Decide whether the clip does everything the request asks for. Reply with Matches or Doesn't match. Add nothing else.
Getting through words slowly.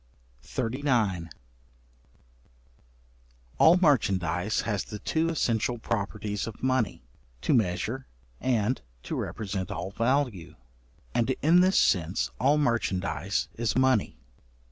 Matches